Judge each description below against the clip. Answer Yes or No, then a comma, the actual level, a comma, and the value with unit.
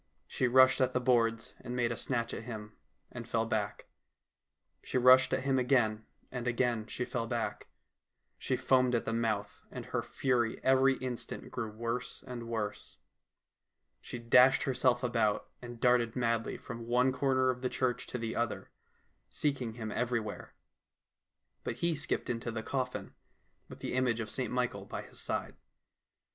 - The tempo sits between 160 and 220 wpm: Yes, average, 165 wpm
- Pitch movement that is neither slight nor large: No, narrow, 1.8 semitones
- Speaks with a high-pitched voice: No, low, 120 Hz